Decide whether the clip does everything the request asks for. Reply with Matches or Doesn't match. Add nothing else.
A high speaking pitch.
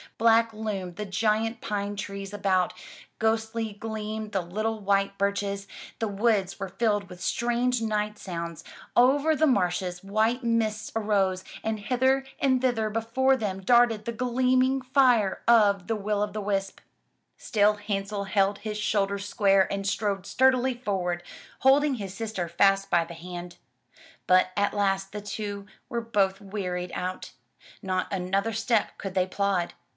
Matches